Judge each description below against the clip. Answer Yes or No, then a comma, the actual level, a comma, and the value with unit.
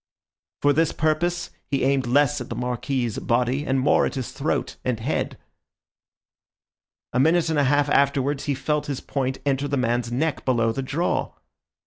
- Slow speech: No, average, 170 wpm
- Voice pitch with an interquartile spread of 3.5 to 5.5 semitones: No, narrow, 2.5 semitones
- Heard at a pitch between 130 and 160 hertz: Yes, low, 135 Hz